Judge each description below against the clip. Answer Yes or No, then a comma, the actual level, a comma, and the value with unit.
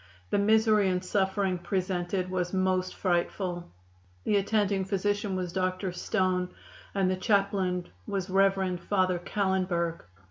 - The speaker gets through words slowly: Yes, slow, 120 wpm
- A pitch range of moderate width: No, narrow, 1.5 semitones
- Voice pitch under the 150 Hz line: No, medium, 185 Hz